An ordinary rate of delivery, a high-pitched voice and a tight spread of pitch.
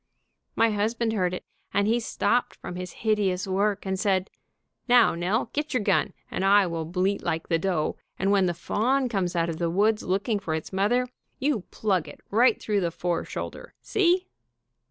No: average, 190 wpm; high, 200 Hz; average, 3.6 semitones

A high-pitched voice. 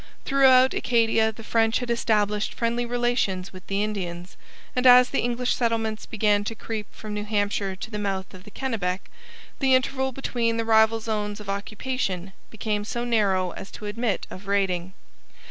Yes: high, 220 Hz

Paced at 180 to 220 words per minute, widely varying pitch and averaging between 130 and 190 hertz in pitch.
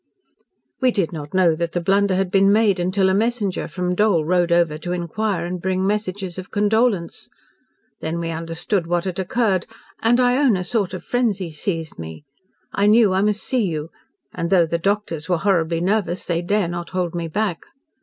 No: average, 195 wpm; average, 3.3 semitones; medium, 185 Hz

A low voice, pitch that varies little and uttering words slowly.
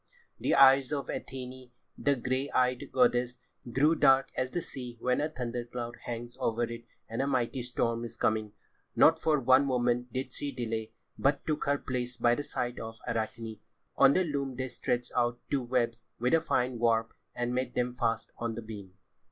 No: low, 125 Hz; narrow, 2.1 semitones; average, 190 wpm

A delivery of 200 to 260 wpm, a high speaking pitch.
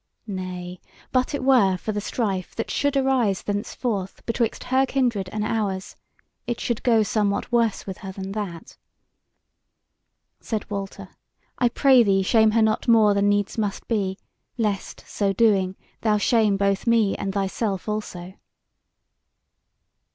No: average, 145 wpm; high, 210 Hz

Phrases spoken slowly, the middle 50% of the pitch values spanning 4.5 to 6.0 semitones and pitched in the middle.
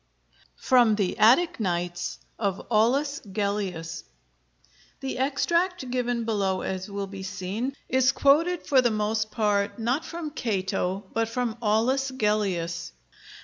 No: slow, 125 wpm; average, 4.8 semitones; high, 220 Hz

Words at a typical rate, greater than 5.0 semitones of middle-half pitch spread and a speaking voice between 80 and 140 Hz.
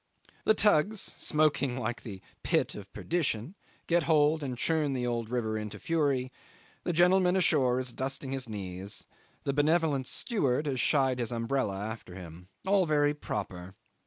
Yes: average, 155 wpm; wide, 5.4 semitones; low, 135 Hz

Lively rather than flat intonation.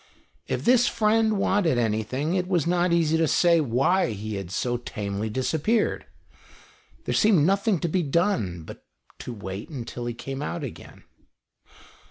Yes: wide, 7.9 semitones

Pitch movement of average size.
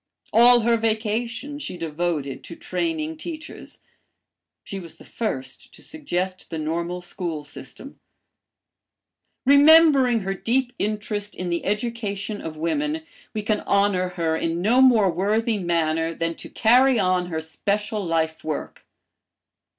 No: wide, 5.8 semitones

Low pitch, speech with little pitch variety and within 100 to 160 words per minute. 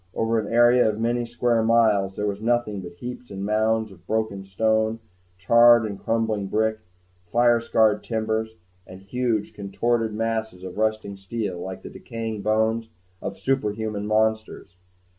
Yes: low, 110 Hz; narrow, 2.0 semitones; average, 150 wpm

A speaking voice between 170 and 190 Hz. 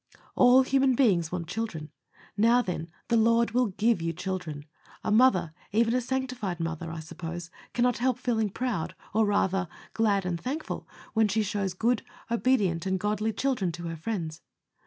No: high, 210 Hz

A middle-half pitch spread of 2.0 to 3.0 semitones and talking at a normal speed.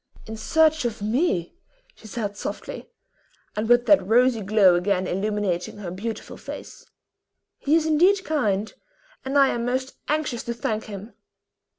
No: average, 5.1 semitones; average, 150 wpm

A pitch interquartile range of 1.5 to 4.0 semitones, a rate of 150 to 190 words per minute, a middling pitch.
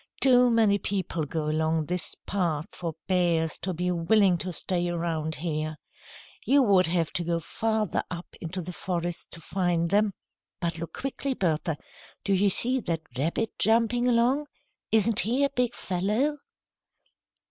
No: average, 4.9 semitones; average, 155 wpm; medium, 180 Hz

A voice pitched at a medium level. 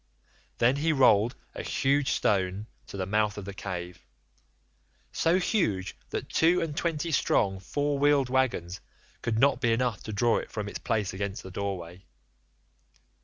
No: low, 110 Hz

